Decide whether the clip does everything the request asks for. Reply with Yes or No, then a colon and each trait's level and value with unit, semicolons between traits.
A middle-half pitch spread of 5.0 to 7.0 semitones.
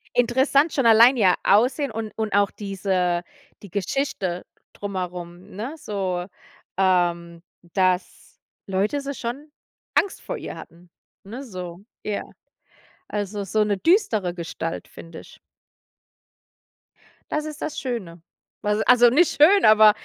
Yes: wide, 5.4 semitones